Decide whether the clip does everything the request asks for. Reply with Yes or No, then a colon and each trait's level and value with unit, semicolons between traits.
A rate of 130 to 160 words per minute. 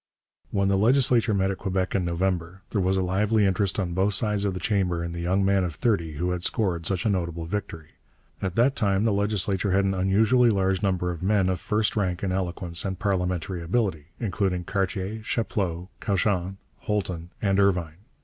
No: average, 195 wpm